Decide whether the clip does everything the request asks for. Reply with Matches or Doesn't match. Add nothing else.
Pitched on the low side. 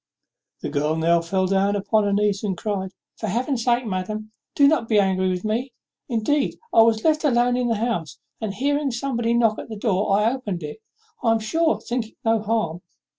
Doesn't match